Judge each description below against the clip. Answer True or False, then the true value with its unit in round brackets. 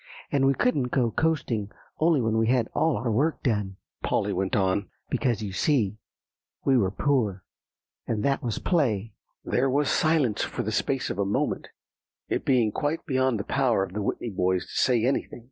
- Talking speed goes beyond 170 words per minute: True (185 wpm)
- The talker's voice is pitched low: True (120 Hz)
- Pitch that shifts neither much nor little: True (4.9 semitones)